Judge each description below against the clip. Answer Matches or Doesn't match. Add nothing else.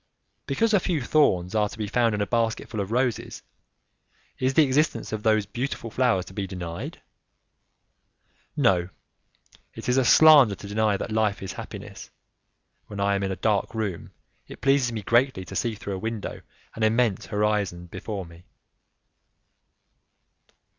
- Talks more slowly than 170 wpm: Matches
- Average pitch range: Matches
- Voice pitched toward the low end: Matches